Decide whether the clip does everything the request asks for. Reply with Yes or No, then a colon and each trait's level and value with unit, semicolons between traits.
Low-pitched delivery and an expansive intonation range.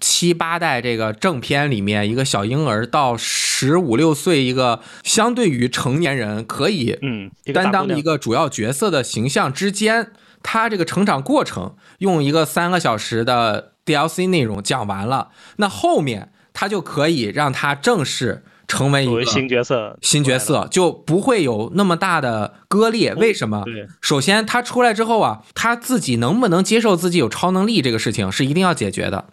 No: medium, 160 Hz; wide, 8.2 semitones